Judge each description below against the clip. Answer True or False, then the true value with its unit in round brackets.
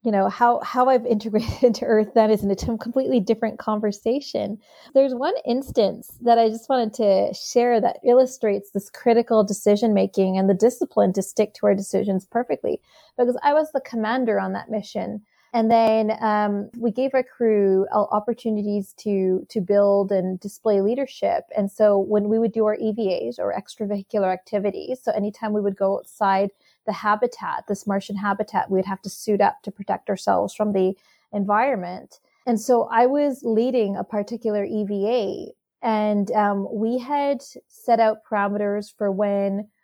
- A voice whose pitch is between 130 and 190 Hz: False (215 Hz)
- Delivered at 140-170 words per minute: True (165 wpm)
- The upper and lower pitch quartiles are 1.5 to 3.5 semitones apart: True (2.8 semitones)